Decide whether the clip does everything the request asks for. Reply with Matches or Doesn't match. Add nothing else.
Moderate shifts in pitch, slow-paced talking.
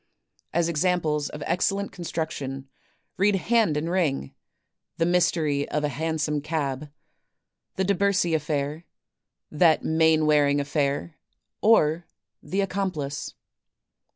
Matches